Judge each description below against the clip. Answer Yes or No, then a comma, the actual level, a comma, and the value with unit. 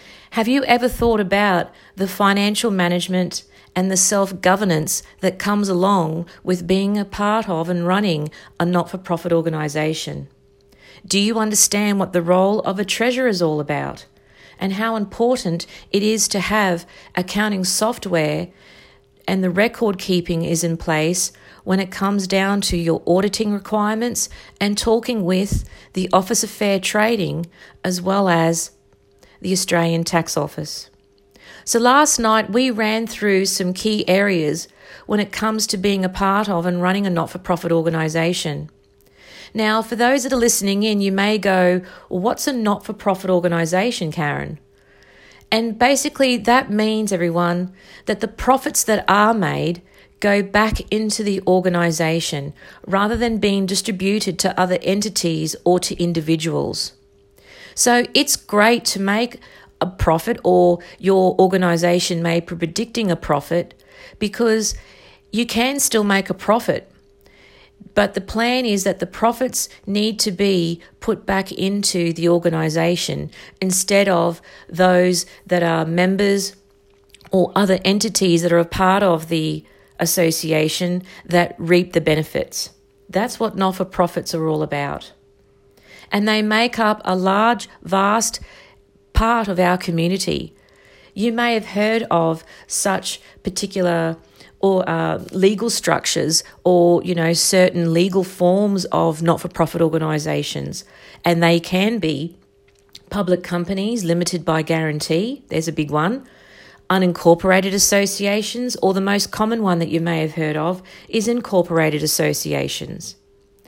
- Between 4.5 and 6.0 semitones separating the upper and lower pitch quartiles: No, average, 3.7 semitones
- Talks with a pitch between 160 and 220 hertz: Yes, medium, 185 Hz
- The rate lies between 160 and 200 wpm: No, average, 140 wpm